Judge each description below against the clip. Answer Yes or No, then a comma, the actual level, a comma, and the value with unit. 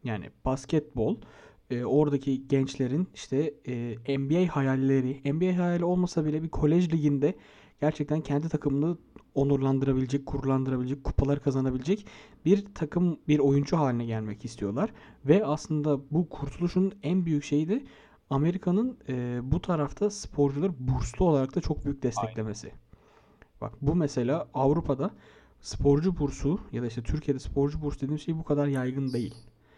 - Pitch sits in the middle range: Yes, medium, 145 Hz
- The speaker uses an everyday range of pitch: Yes, average, 3.2 semitones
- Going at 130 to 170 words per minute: Yes, average, 135 wpm